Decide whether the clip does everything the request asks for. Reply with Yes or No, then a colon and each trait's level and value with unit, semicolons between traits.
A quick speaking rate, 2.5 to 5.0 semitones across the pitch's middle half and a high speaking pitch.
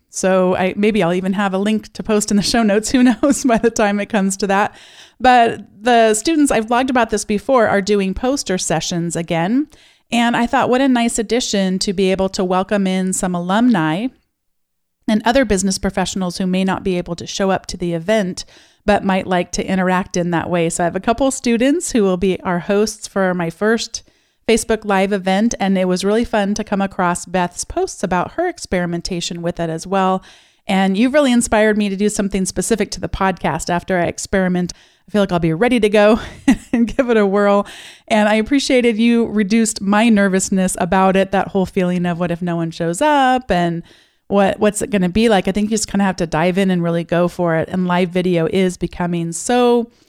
Yes: fast, 220 wpm; average, 3.6 semitones; high, 200 Hz